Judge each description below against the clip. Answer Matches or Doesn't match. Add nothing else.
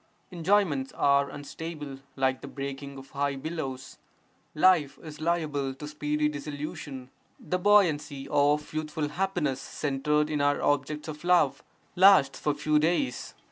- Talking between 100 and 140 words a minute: Matches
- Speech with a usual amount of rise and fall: Doesn't match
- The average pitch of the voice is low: Doesn't match